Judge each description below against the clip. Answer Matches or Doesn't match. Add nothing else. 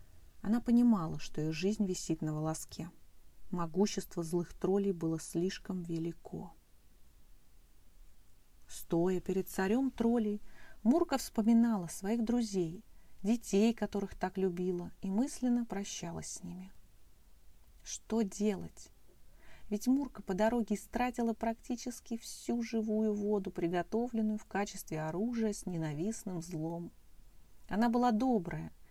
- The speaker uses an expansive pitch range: Matches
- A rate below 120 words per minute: Matches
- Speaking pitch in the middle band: Doesn't match